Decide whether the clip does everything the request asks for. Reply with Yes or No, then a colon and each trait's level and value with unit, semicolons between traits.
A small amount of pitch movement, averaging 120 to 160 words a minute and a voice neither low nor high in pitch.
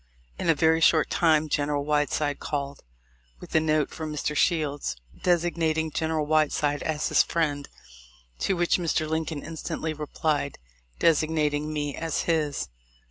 Yes: narrow, 1.6 semitones; average, 140 wpm; medium, 155 Hz